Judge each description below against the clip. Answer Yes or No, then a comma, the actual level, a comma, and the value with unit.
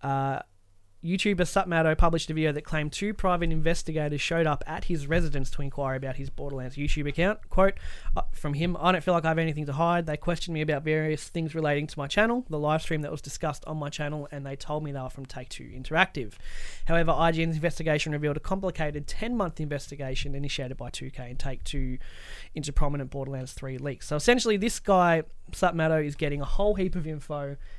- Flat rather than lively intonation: No, average, 3.1 semitones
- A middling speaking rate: No, fast, 210 wpm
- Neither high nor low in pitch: Yes, medium, 150 Hz